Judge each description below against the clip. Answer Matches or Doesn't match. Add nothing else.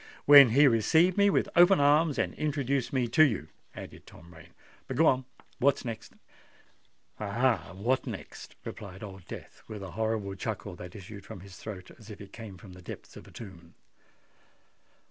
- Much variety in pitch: Matches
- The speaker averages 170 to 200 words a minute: Matches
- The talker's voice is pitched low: Matches